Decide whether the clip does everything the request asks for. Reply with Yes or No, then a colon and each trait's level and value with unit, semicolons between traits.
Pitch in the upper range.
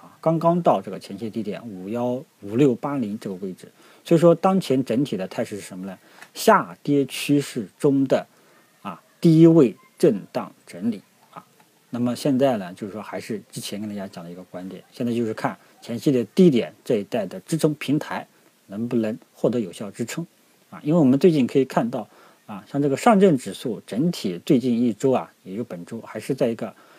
No: low, 135 Hz